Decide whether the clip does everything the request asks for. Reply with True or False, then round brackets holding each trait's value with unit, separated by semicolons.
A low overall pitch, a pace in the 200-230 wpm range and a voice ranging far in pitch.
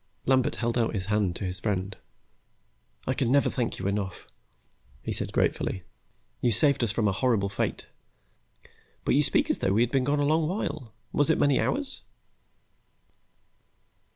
False (115 Hz; 170 wpm; 5.8 semitones)